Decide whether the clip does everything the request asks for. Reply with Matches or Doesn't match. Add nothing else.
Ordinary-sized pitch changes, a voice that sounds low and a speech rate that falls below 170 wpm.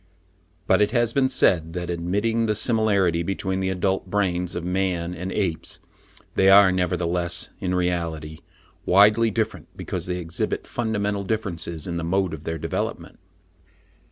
Matches